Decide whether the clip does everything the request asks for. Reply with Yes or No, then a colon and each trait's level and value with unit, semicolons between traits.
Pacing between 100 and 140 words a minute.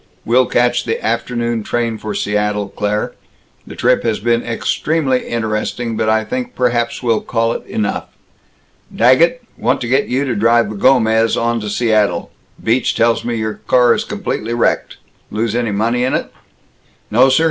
No: average, 170 wpm